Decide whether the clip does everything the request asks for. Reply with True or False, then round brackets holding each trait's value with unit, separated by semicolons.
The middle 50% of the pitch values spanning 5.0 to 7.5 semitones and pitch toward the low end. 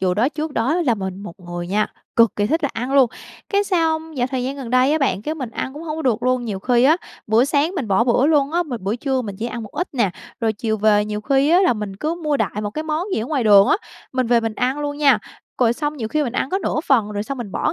False (5.4 semitones; 255 Hz)